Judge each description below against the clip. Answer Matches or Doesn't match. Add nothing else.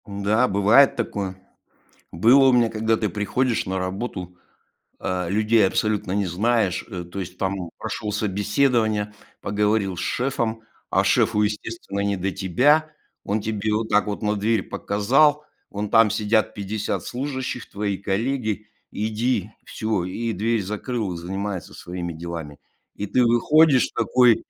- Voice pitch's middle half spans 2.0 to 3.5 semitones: Matches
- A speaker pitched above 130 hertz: Doesn't match